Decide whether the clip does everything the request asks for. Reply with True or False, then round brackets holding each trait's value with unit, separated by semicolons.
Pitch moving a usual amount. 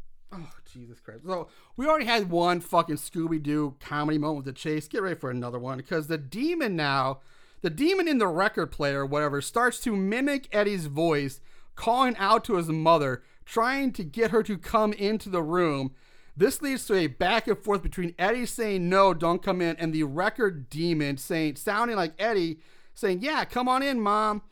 False (6.4 semitones)